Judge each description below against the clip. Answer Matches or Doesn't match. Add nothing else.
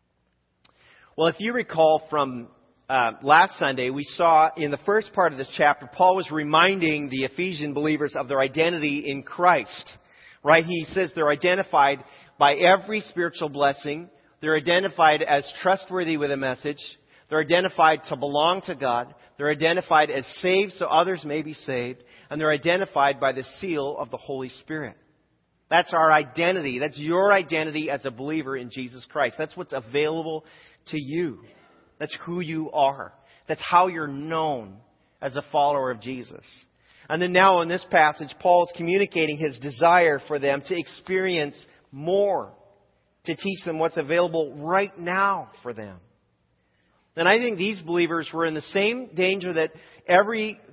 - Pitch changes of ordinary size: Matches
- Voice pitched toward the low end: Doesn't match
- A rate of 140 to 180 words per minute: Matches